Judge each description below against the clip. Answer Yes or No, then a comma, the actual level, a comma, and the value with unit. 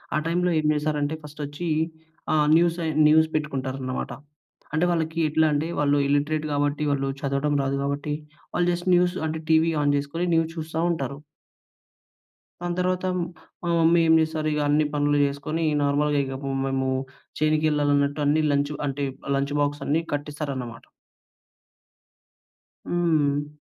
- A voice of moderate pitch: Yes, medium, 150 Hz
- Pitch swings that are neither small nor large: No, narrow, 2.0 semitones